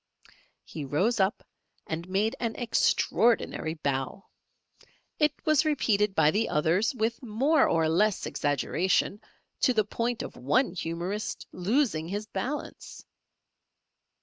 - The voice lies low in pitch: No, high, 205 Hz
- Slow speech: Yes, slow, 120 wpm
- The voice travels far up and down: Yes, wide, 6.0 semitones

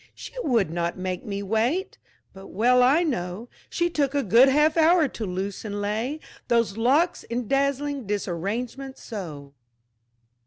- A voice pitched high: Yes, high, 235 Hz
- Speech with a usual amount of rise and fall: No, wide, 6.0 semitones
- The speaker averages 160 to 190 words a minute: No, average, 150 wpm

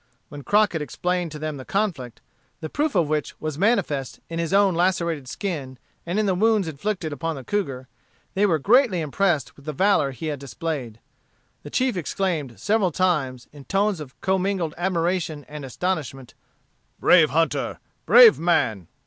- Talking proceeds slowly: No, average, 165 wpm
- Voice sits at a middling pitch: Yes, medium, 165 Hz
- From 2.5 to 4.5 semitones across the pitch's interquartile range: No, average, 5.0 semitones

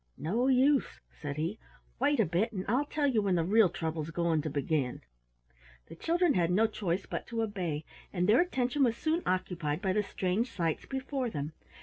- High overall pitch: Yes, high, 195 Hz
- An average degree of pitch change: No, wide, 7.1 semitones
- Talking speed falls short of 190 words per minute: No, average, 195 wpm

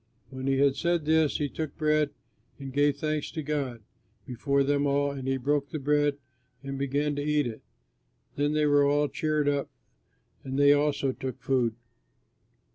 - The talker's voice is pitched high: No, medium, 145 Hz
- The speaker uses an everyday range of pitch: No, narrow, 1.5 semitones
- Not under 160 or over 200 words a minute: Yes, average, 175 wpm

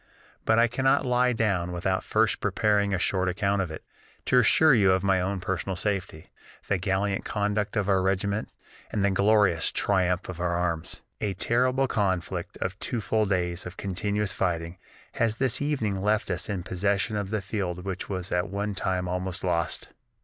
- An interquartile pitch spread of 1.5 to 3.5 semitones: Yes, narrow, 2.5 semitones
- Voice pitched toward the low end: Yes, low, 100 Hz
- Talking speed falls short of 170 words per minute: No, average, 180 wpm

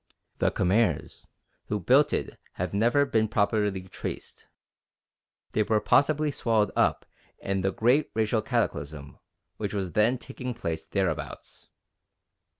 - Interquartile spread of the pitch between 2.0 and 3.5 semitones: No, average, 3.9 semitones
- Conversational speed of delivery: No, slow, 125 wpm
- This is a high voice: No, low, 110 Hz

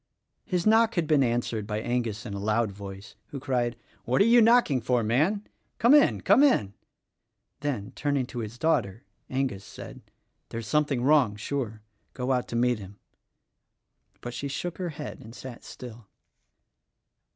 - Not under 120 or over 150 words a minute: No, average, 165 wpm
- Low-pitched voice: Yes, low, 125 Hz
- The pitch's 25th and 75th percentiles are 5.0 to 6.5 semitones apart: Yes, average, 5.3 semitones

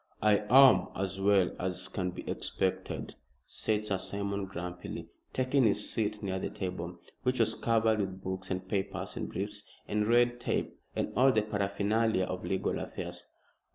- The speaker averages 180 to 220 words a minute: No, average, 160 wpm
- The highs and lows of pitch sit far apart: No, average, 2.9 semitones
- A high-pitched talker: No, low, 100 Hz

